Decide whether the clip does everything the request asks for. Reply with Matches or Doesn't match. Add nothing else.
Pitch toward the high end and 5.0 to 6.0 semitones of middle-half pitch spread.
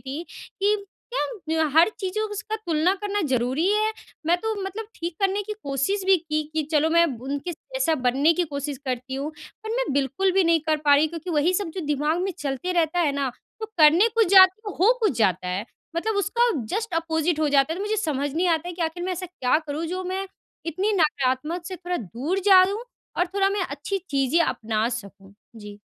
Matches